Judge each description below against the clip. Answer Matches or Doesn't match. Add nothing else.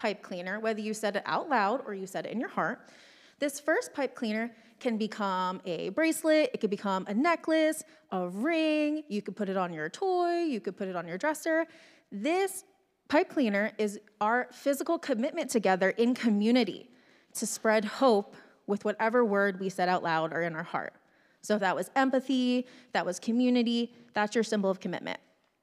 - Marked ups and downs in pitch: Matches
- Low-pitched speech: Doesn't match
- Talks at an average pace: Matches